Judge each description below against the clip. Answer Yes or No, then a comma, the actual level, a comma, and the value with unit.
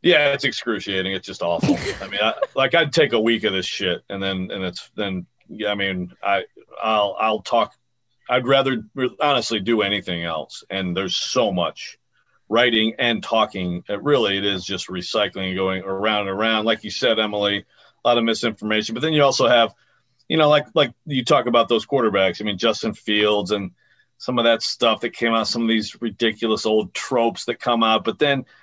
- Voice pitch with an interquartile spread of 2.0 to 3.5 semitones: Yes, average, 3.2 semitones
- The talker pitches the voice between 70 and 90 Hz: No, low, 110 Hz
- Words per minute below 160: No, fast, 205 wpm